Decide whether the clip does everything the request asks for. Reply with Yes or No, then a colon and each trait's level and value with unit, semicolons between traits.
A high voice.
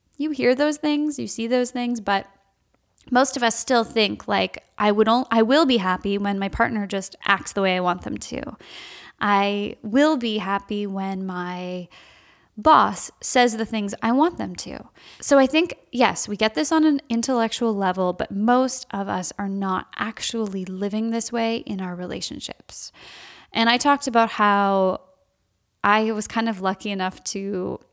Yes: high, 220 Hz